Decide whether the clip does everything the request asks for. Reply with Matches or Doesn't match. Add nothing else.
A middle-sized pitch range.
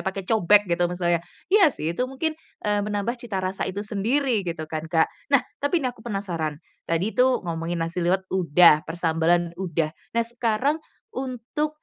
Doesn't match